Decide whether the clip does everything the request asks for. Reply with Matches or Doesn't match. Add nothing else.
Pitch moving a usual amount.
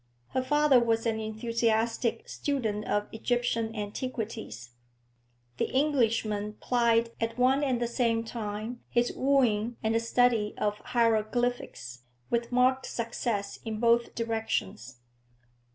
Doesn't match